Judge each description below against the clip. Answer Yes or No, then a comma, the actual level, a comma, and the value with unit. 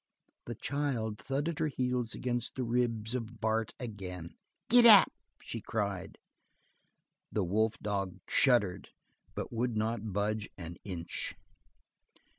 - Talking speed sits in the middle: No, slow, 115 wpm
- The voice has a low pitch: Yes, low, 115 Hz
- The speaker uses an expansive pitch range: No, average, 3.4 semitones